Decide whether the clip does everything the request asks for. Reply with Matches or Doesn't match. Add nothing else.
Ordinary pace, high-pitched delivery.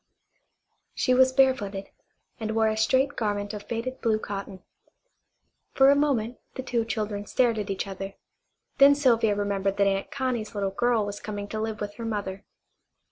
Matches